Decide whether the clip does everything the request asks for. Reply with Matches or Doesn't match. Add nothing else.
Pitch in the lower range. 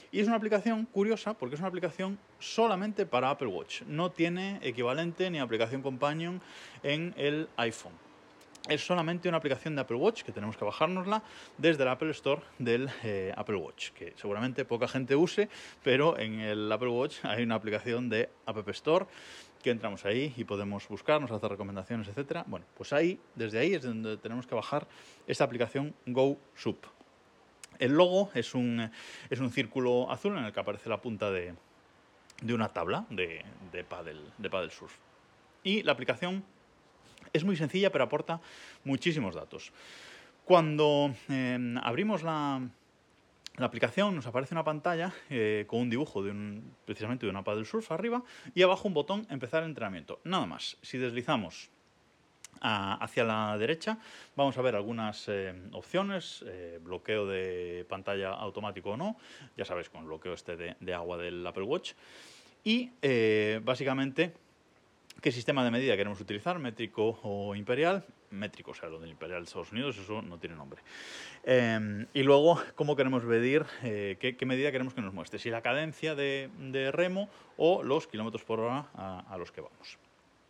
Matches